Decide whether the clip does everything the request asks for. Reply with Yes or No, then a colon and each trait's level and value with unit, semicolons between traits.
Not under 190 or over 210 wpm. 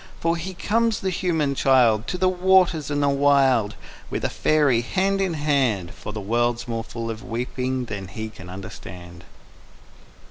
No: average, 170 wpm